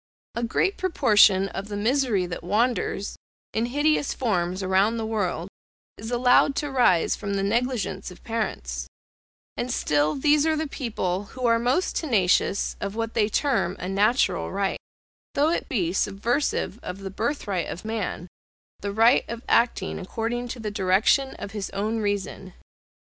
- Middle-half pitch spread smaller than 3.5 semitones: No, average, 4.2 semitones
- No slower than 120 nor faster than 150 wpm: No, average, 160 wpm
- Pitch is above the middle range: Yes, high, 220 Hz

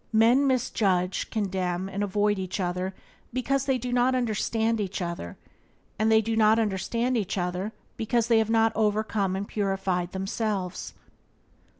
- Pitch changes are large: No, average, 3.1 semitones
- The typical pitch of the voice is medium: No, high, 210 Hz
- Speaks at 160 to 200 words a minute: No, average, 150 wpm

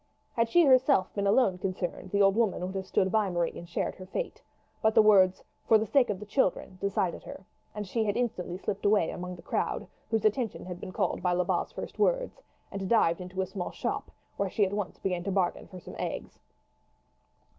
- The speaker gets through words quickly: Yes, fast, 215 wpm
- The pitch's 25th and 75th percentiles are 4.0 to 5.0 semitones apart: No, average, 3.0 semitones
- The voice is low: No, high, 195 Hz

